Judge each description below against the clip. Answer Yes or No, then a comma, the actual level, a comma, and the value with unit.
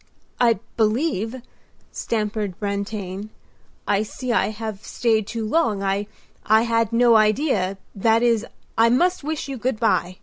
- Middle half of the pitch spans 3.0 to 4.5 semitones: No, narrow, 2.5 semitones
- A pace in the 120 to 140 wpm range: Yes, slow, 135 wpm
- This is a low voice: No, high, 220 Hz